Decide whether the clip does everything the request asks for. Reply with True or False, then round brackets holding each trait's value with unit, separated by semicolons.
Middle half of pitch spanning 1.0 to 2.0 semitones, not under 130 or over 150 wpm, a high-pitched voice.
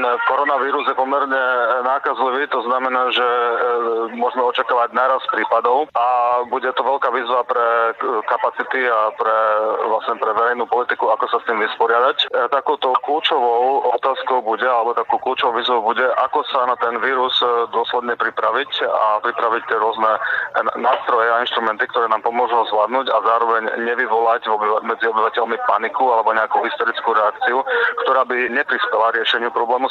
False (1.7 semitones; 145 wpm; 115 Hz)